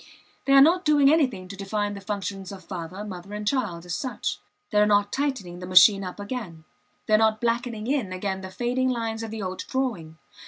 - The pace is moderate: No, fast, 210 wpm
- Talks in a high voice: Yes, high, 210 Hz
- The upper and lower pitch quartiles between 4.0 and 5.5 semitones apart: Yes, average, 4.7 semitones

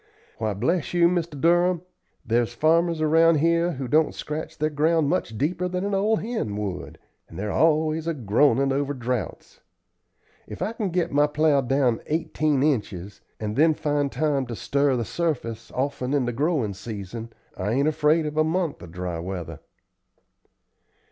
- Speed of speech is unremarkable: Yes, average, 165 wpm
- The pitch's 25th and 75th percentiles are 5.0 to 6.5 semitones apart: Yes, wide, 5.6 semitones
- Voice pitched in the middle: Yes, medium, 145 Hz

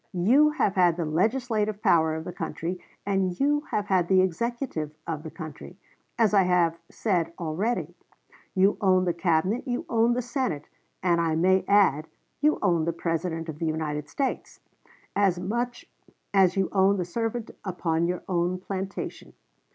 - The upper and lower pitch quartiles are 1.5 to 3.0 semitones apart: No, average, 4.1 semitones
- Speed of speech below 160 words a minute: No, average, 165 wpm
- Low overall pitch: No, medium, 185 Hz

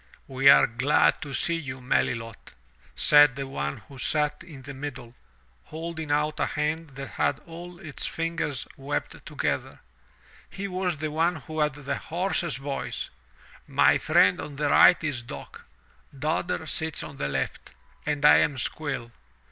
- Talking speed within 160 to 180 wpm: Yes, average, 165 wpm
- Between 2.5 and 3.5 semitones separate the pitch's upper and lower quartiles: Yes, average, 2.9 semitones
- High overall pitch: No, medium, 145 Hz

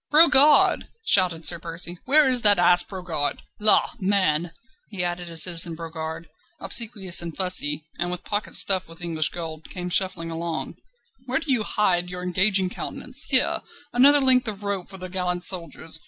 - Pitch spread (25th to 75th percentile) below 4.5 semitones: Yes, average, 3.4 semitones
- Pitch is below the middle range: No, medium, 180 Hz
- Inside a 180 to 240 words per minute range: No, average, 170 wpm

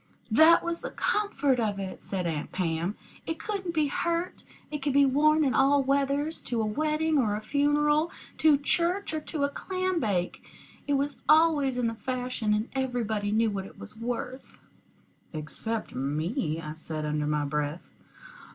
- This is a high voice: Yes, very high, 260 Hz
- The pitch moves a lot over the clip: Yes, wide, 6.9 semitones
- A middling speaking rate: Yes, average, 170 wpm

